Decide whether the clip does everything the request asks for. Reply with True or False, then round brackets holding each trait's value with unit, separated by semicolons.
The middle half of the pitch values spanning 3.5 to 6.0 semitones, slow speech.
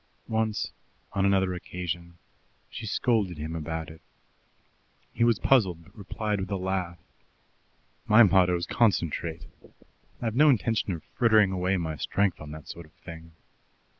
False (4.2 semitones; 145 wpm)